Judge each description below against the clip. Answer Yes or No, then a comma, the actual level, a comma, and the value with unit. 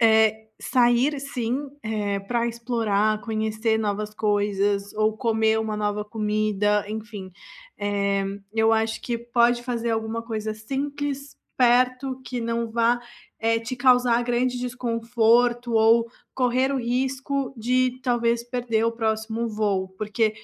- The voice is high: Yes, high, 230 Hz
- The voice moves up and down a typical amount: No, narrow, 2.1 semitones